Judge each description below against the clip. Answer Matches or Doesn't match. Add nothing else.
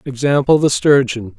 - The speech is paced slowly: Matches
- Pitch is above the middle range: Doesn't match